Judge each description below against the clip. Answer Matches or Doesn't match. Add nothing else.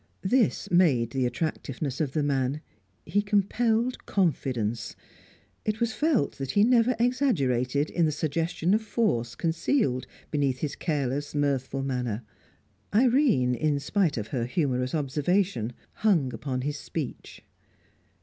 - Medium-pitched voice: Matches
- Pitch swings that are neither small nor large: Doesn't match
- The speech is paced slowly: Matches